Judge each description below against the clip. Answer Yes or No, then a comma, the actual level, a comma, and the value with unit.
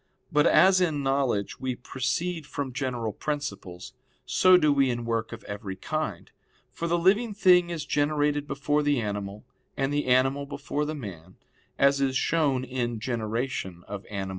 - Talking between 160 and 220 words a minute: Yes, average, 165 wpm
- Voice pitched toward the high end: No, low, 135 Hz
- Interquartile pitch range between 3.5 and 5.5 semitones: Yes, average, 4.3 semitones